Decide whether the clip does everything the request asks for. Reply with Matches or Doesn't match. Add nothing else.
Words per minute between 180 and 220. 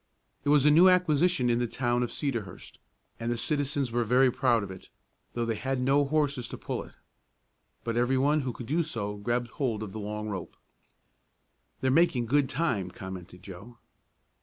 Matches